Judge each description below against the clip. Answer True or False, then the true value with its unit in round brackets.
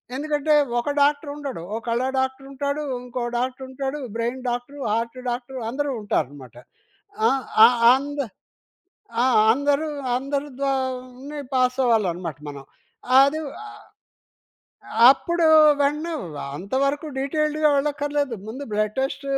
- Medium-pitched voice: False (270 Hz)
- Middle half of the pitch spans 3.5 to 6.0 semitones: False (3.1 semitones)